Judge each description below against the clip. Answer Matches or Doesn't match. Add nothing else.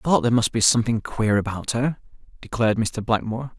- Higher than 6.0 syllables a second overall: Matches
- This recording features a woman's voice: Doesn't match